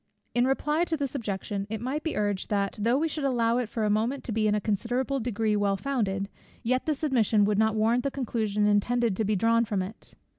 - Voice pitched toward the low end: No, high, 225 Hz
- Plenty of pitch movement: No, average, 3.6 semitones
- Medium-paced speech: No, fast, 230 wpm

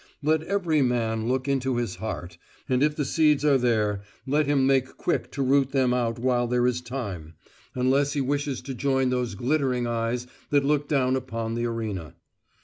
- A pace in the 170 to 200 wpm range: Yes, average, 185 wpm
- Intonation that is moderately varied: Yes, average, 3.0 semitones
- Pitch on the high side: No, low, 130 Hz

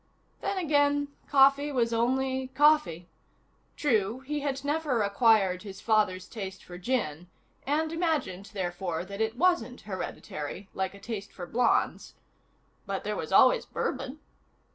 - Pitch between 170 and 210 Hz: No, high, 230 Hz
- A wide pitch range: Yes, wide, 6.9 semitones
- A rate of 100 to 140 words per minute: Yes, slow, 135 wpm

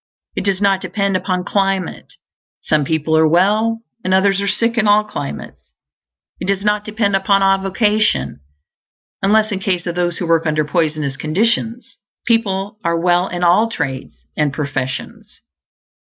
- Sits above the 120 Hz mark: Yes, high, 190 Hz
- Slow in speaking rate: No, average, 155 wpm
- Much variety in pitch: No, average, 4.1 semitones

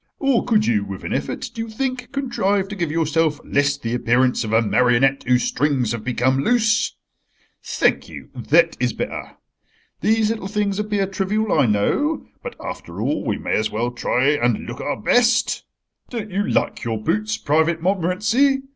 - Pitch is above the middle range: No, medium, 165 Hz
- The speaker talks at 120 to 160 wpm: No, average, 175 wpm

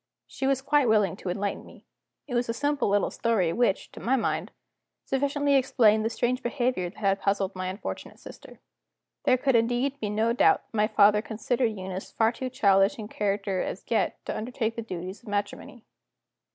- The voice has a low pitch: No, high, 225 Hz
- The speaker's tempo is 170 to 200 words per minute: Yes, average, 190 wpm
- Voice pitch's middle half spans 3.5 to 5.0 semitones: Yes, average, 4.0 semitones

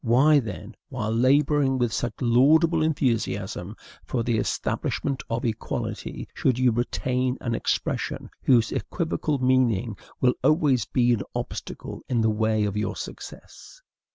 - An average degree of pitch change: Yes, average, 3.1 semitones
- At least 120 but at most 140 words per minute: Yes, slow, 135 wpm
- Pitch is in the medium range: No, low, 125 Hz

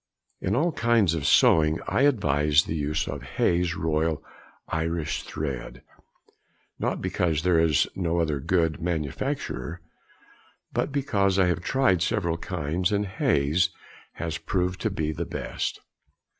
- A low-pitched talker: Yes, very low, 85 Hz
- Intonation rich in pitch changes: No, average, 3.3 semitones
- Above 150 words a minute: No, average, 140 wpm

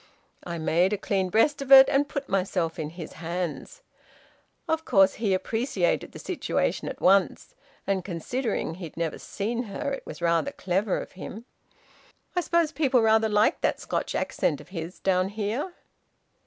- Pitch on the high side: Yes, high, 200 Hz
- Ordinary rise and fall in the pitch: No, wide, 6.3 semitones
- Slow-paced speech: No, average, 165 wpm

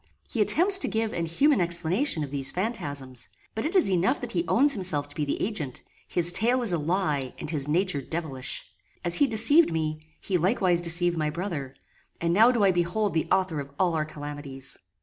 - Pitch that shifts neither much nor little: No, wide, 5.8 semitones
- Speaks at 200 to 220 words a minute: Yes, fast, 205 wpm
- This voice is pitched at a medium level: Yes, medium, 175 Hz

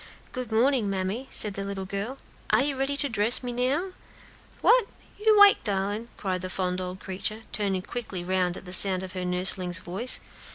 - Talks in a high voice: Yes, high, 200 Hz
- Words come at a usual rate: Yes, average, 190 wpm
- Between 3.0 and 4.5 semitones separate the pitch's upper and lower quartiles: No, average, 5.1 semitones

